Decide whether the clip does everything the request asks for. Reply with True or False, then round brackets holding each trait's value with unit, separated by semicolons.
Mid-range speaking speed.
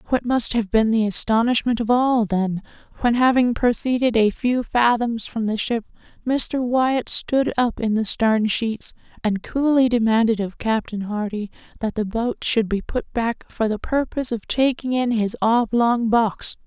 True (175 wpm)